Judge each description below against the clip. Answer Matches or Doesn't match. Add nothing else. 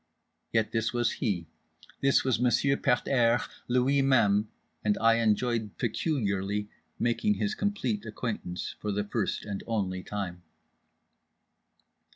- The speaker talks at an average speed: Doesn't match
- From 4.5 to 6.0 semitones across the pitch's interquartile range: Doesn't match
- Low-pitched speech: Matches